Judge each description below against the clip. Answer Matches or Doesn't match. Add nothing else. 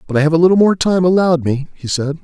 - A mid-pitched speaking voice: Matches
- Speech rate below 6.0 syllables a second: Doesn't match